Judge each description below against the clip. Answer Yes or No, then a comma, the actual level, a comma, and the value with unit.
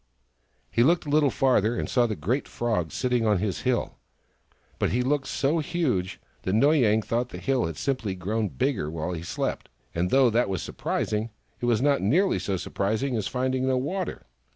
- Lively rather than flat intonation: No, average, 4.6 semitones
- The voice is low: Yes, low, 120 Hz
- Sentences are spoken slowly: No, average, 195 wpm